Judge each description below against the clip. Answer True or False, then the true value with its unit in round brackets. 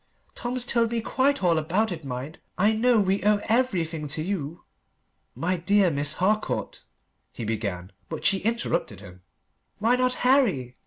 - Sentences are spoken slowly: False (155 wpm)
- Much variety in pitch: True (7.5 semitones)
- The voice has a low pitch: False (190 Hz)